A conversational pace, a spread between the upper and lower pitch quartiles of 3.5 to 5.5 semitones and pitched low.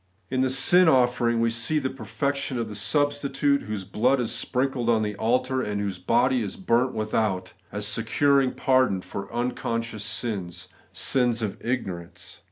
Yes: average, 165 wpm; average, 3.8 semitones; low, 120 Hz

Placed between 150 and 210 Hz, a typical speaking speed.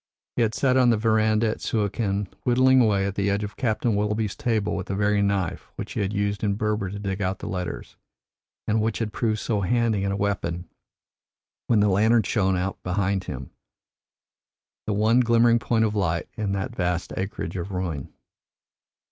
No: low, 105 Hz; average, 185 wpm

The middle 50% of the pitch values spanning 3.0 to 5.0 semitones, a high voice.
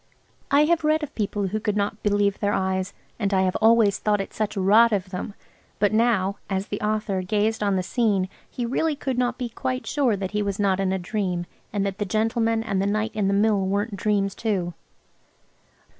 No: narrow, 2.4 semitones; high, 205 Hz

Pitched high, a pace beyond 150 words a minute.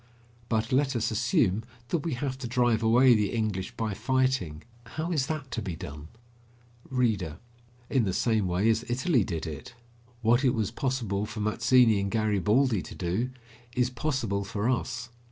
No: low, 115 Hz; average, 170 wpm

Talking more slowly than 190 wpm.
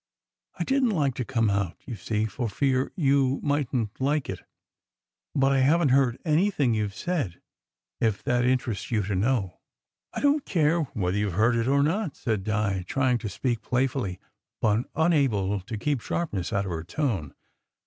No: average, 195 wpm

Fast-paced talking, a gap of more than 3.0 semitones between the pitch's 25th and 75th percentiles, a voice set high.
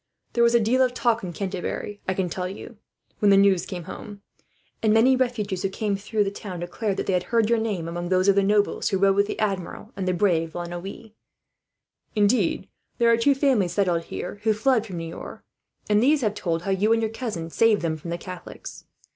Yes: fast, 225 wpm; average, 3.5 semitones; high, 200 Hz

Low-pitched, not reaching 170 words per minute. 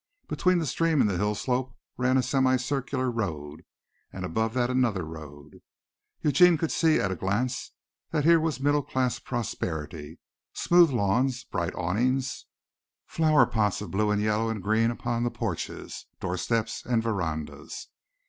Yes: low, 115 Hz; average, 155 wpm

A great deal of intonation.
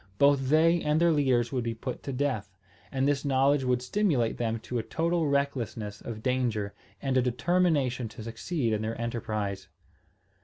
No: average, 3.9 semitones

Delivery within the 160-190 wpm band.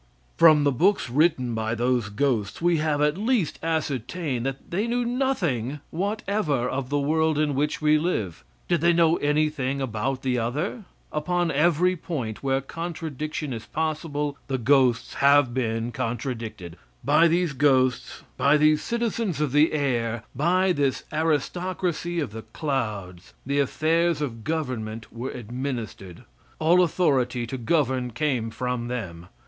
No: average, 145 wpm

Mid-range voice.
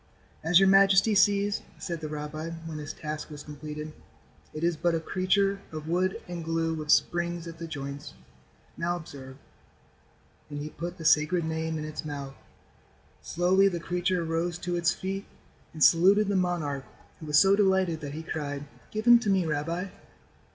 Yes: medium, 165 Hz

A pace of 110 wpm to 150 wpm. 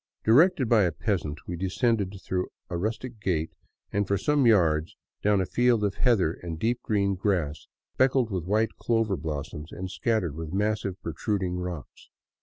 No: average, 165 wpm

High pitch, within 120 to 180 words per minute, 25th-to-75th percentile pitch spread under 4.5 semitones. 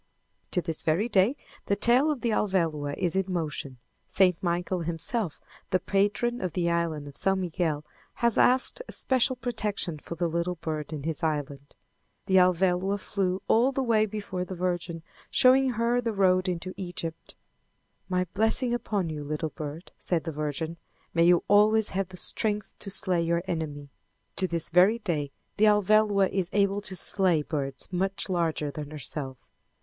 No: medium, 180 Hz; average, 170 wpm; average, 4.1 semitones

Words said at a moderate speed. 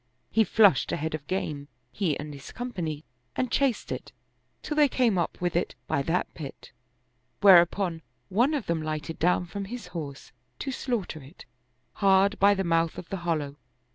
Yes: average, 180 wpm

